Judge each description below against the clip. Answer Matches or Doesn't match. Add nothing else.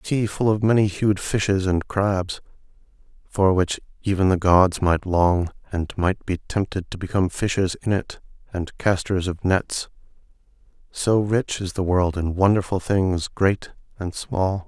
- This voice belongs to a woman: Doesn't match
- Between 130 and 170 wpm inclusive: Matches